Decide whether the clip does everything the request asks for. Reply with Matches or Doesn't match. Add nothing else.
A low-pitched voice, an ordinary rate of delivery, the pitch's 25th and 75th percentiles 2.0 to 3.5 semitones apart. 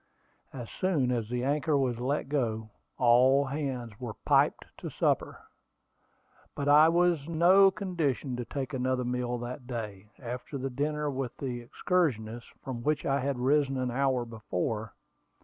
Matches